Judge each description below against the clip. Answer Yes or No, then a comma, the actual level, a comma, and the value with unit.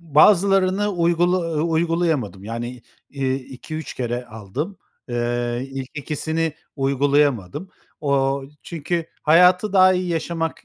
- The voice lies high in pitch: No, medium, 150 Hz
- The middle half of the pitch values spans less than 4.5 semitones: No, average, 5.1 semitones